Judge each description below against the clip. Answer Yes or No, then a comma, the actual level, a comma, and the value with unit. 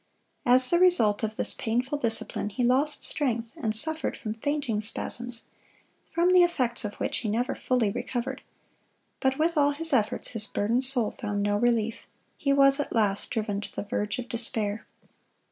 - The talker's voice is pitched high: Yes, high, 240 Hz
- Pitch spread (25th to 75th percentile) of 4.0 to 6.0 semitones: Yes, average, 4.3 semitones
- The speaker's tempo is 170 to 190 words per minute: Yes, average, 180 wpm